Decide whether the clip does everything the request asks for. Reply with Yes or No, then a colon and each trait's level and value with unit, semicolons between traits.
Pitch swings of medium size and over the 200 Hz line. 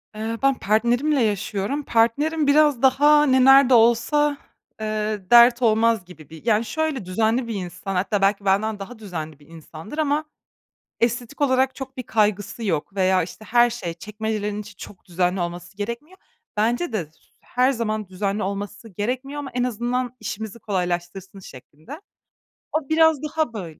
Yes: average, 4.9 semitones; high, 220 Hz